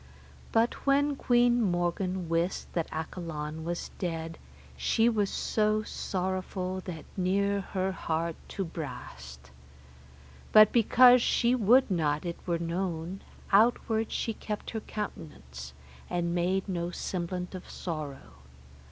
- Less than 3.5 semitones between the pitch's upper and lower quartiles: No, average, 4.2 semitones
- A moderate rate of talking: No, slow, 120 wpm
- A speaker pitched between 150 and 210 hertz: Yes, medium, 185 Hz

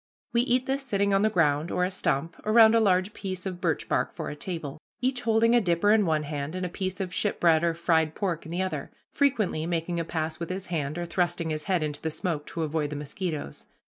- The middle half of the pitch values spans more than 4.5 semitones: No, average, 4.0 semitones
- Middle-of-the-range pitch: Yes, medium, 175 Hz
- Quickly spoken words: Yes, fast, 245 wpm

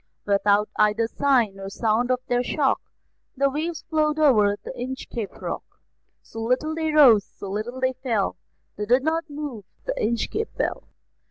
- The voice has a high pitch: Yes, very high, 250 Hz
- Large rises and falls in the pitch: Yes, wide, 5.7 semitones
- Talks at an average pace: Yes, average, 160 wpm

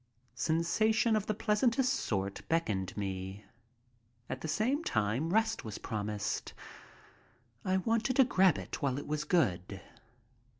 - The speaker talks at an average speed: No, slow, 130 wpm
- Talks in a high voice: No, medium, 160 Hz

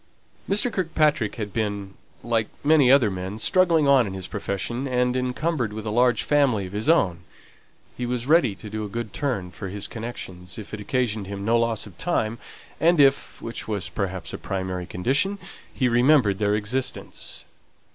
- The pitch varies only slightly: No, average, 4.7 semitones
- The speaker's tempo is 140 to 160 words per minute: No, average, 175 wpm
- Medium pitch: No, low, 115 Hz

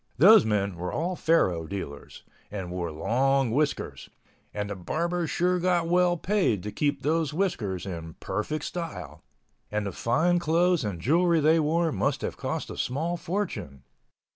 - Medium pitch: Yes, medium, 145 Hz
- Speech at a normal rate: Yes, average, 150 wpm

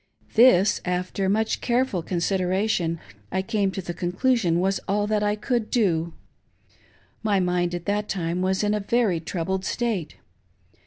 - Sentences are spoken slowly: No, average, 155 wpm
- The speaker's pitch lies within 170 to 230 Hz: Yes, high, 190 Hz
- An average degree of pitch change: Yes, average, 3.1 semitones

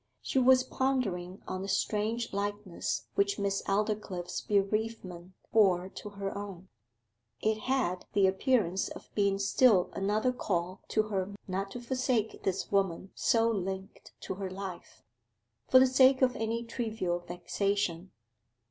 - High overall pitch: Yes, high, 200 Hz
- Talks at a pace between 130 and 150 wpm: Yes, average, 140 wpm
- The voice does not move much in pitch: No, average, 3.1 semitones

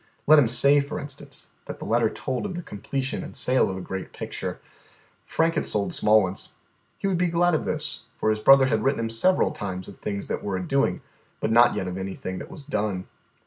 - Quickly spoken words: Yes, fast, 225 wpm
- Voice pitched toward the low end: Yes, low, 120 Hz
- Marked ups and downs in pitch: Yes, wide, 6.6 semitones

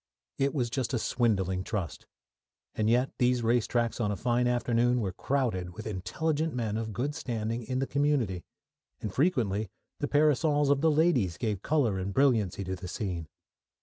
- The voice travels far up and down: No, average, 5.0 semitones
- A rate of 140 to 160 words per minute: No, average, 175 wpm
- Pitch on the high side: No, low, 120 Hz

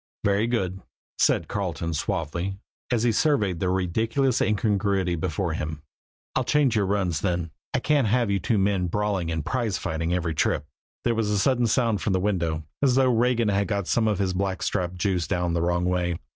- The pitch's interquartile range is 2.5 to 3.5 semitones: No, average, 4.1 semitones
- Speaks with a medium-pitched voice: No, low, 100 Hz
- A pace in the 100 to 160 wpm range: No, average, 190 wpm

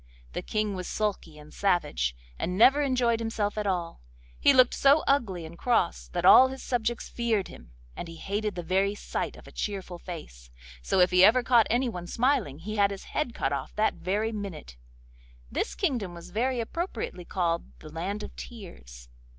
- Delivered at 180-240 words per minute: Yes, average, 185 wpm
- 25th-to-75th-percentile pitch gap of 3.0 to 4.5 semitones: No, wide, 5.5 semitones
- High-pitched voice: Yes, high, 200 Hz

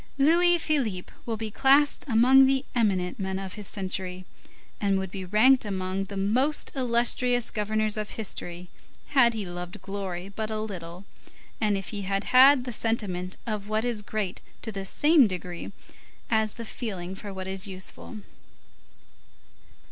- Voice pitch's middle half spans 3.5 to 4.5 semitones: Yes, average, 3.9 semitones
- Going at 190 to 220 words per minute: No, average, 155 wpm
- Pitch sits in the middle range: No, high, 210 Hz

